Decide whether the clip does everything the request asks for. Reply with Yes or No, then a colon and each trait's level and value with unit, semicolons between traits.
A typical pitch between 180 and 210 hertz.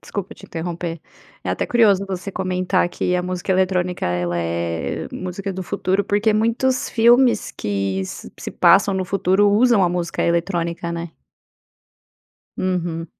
Yes: medium, 185 Hz